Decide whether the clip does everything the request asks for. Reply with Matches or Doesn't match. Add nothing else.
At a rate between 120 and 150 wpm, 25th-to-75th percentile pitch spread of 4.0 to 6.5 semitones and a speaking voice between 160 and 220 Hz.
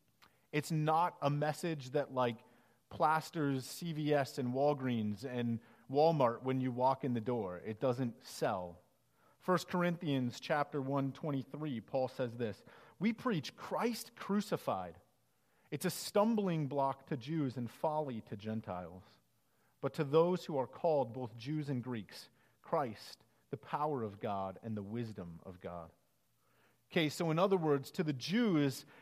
Doesn't match